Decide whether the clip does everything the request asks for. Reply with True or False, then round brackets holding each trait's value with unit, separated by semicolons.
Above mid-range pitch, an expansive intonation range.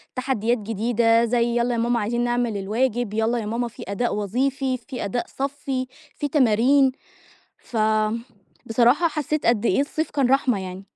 False (240 Hz; 2.8 semitones)